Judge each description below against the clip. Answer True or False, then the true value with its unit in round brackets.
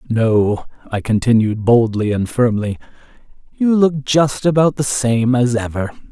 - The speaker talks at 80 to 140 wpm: True (135 wpm)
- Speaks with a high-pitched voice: False (120 Hz)